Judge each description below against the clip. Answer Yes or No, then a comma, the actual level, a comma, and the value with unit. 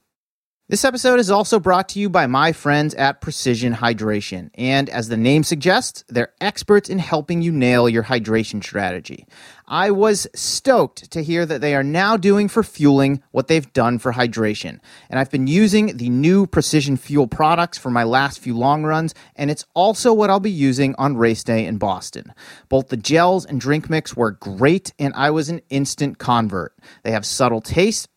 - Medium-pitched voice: Yes, medium, 145 Hz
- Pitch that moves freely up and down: Yes, wide, 6.4 semitones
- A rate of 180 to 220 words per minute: Yes, average, 190 wpm